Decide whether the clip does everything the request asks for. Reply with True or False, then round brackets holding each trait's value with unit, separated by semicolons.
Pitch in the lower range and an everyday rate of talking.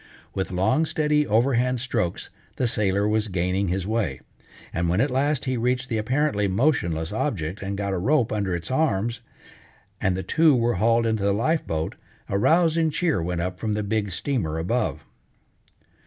True (110 Hz; 175 wpm)